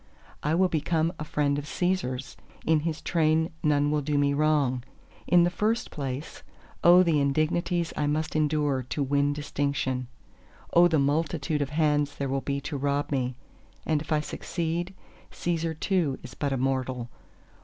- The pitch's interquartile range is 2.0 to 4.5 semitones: Yes, narrow, 2.5 semitones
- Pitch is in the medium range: Yes, medium, 150 Hz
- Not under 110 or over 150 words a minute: No, average, 165 wpm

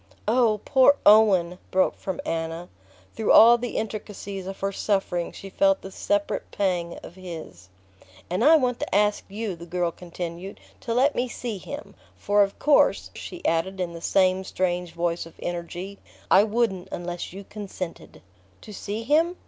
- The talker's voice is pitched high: Yes, high, 195 Hz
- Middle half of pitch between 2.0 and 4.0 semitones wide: Yes, average, 3.7 semitones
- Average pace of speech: Yes, average, 165 wpm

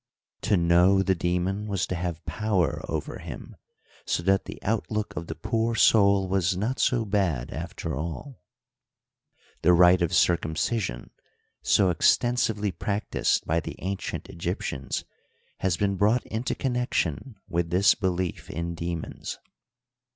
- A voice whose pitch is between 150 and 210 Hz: No, very low, 95 Hz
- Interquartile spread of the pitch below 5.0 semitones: Yes, average, 3.5 semitones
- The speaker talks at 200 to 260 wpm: No, slow, 135 wpm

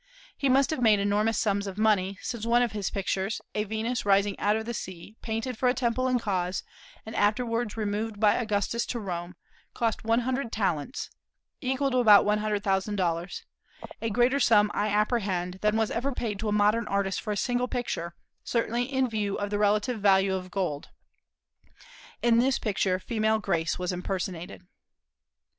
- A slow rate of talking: No, average, 180 wpm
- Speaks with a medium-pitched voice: No, high, 210 Hz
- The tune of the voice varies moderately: Yes, average, 3.1 semitones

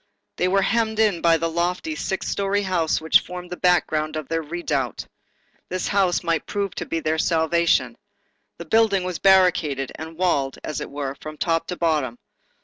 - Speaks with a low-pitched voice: No, medium, 170 Hz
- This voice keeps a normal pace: Yes, average, 170 wpm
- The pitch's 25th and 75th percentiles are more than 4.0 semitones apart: No, average, 2.9 semitones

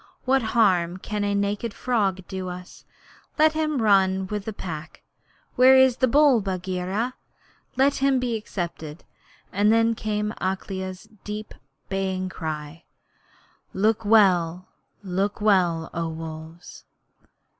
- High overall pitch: Yes, high, 195 Hz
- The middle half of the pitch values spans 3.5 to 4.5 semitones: Yes, average, 3.8 semitones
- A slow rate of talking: Yes, slow, 125 wpm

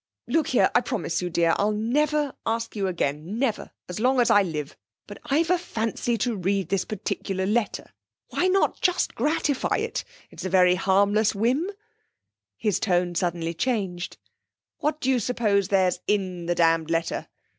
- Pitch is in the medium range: No, high, 205 Hz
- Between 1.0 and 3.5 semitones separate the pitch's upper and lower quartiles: No, wide, 5.5 semitones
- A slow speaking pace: No, average, 165 wpm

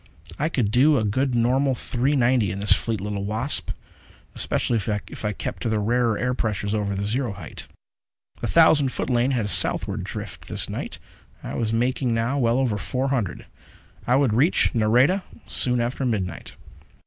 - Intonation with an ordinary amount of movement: Yes, average, 3.8 semitones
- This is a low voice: Yes, low, 120 Hz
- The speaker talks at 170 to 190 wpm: Yes, average, 180 wpm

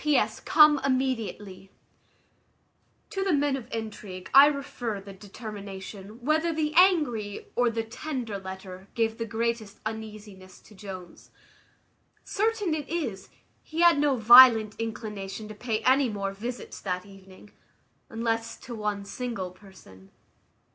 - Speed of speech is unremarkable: No, slow, 130 wpm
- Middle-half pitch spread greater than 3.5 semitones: Yes, average, 4.9 semitones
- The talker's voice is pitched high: Yes, high, 225 Hz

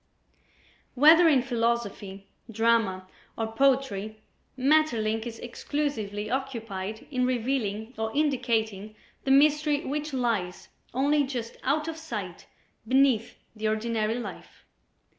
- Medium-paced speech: No, slow, 105 wpm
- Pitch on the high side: Yes, high, 235 Hz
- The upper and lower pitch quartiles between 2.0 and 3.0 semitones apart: No, average, 4.1 semitones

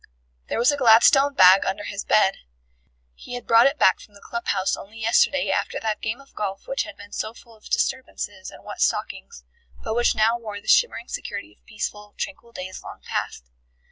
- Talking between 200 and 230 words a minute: Yes, fast, 205 wpm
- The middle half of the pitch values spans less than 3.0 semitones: No, average, 3.3 semitones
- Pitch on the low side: No, high, 220 Hz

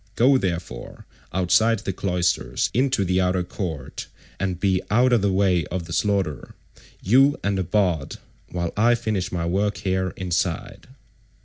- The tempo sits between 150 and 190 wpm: No, average, 140 wpm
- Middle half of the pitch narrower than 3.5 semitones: Yes, average, 2.8 semitones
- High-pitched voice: No, very low, 95 Hz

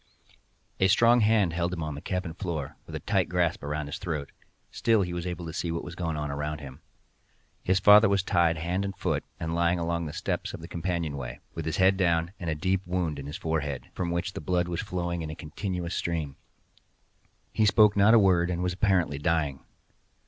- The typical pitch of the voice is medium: No, very low, 85 Hz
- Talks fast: Yes, fast, 220 wpm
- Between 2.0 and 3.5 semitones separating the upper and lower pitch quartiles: Yes, average, 2.8 semitones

